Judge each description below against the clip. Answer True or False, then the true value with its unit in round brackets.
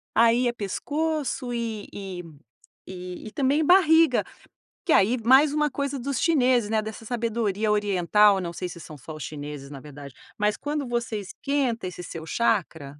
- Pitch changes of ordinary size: False (6.7 semitones)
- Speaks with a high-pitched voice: True (225 Hz)